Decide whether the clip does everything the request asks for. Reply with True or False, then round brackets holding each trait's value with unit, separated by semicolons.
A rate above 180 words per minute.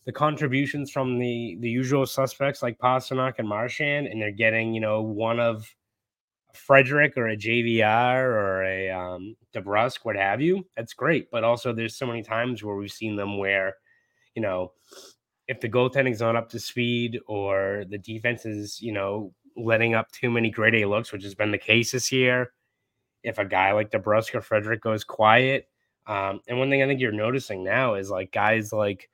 True (190 wpm)